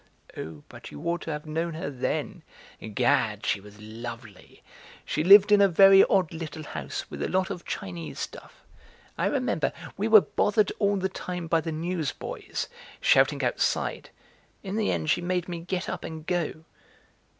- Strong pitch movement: No, average, 4.8 semitones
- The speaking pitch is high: No, medium, 165 Hz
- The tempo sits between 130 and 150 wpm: No, average, 170 wpm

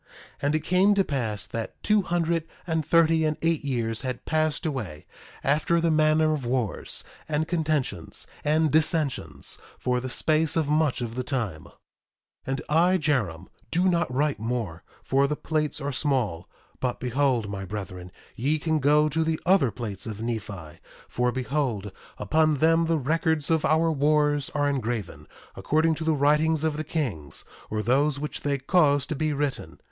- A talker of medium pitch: Yes, medium, 145 Hz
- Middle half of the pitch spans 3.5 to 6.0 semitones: Yes, average, 4.5 semitones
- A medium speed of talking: Yes, average, 170 wpm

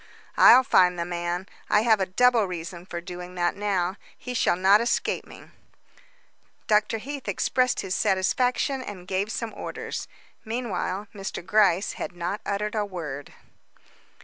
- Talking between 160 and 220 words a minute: No, average, 150 wpm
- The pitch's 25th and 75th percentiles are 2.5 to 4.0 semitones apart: Yes, average, 3.6 semitones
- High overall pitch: Yes, high, 195 Hz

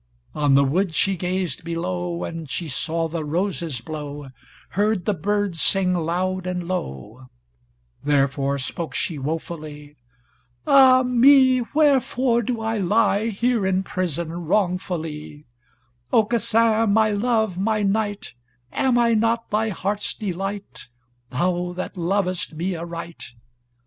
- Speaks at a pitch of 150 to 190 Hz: Yes, medium, 185 Hz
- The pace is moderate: No, slow, 125 wpm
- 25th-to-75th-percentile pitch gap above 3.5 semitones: Yes, average, 4.8 semitones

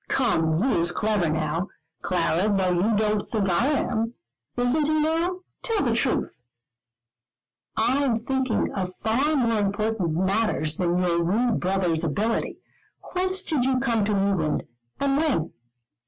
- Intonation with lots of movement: Yes, wide, 6.3 semitones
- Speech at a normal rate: Yes, average, 145 wpm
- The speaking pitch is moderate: No, high, 215 Hz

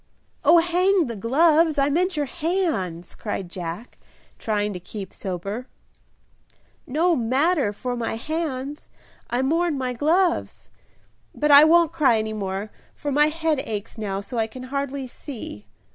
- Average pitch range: No, wide, 6.6 semitones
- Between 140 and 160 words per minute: Yes, average, 145 wpm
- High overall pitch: Yes, very high, 265 Hz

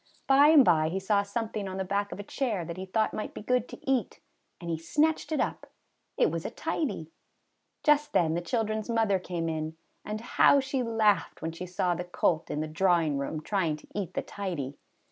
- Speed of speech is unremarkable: No, fast, 215 wpm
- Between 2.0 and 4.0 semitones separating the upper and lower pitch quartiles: No, average, 5.2 semitones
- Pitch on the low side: No, high, 195 Hz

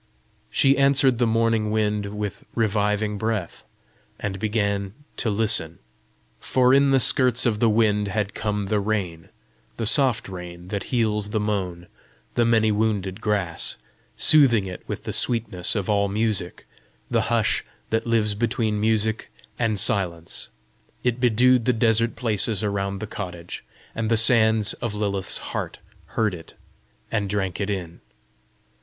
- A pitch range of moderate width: No, narrow, 2.3 semitones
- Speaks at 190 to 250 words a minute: No, average, 145 wpm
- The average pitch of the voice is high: No, low, 105 Hz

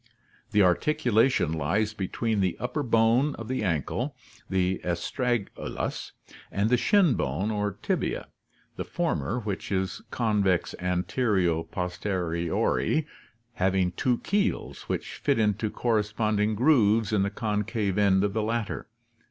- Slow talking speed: Yes, slow, 130 wpm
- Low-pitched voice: Yes, low, 105 Hz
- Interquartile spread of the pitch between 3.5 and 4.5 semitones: Yes, average, 3.8 semitones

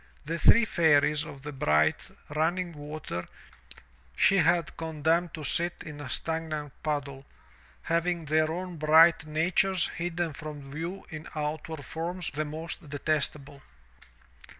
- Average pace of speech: No, slow, 125 wpm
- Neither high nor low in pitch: Yes, medium, 155 Hz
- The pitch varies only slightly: Yes, narrow, 2.3 semitones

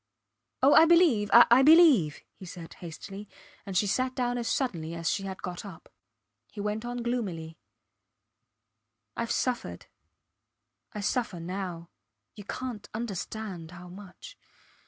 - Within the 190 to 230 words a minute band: No, slow, 135 wpm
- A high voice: Yes, high, 205 Hz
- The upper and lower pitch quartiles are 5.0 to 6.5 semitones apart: Yes, average, 5.3 semitones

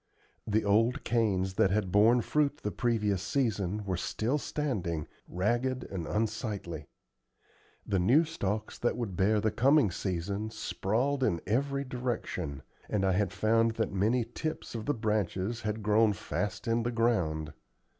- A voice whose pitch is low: Yes, low, 110 Hz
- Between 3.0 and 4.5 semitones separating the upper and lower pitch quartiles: Yes, average, 3.7 semitones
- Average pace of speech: Yes, average, 150 wpm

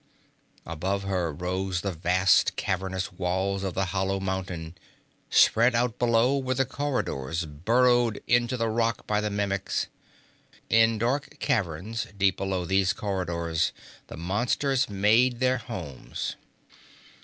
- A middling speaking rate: No, slow, 125 wpm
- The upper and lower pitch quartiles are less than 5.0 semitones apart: Yes, average, 4.3 semitones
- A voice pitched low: Yes, low, 100 Hz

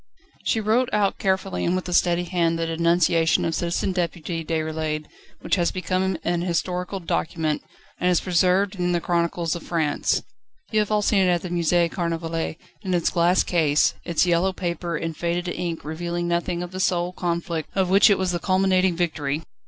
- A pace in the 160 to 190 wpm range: Yes, average, 185 wpm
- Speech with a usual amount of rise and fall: No, narrow, 1.8 semitones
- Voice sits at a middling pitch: Yes, medium, 175 Hz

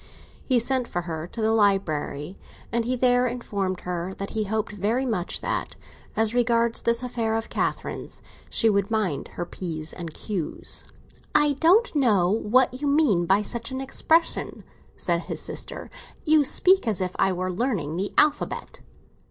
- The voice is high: Yes, high, 220 Hz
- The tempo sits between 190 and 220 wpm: No, average, 165 wpm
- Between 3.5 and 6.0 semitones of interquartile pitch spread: Yes, average, 5.3 semitones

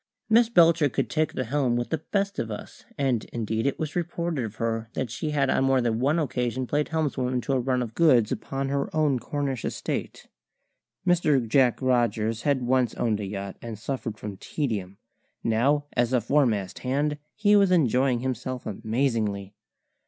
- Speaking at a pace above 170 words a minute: Yes, average, 180 wpm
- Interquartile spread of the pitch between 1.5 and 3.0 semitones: No, average, 4.2 semitones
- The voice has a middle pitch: No, low, 130 Hz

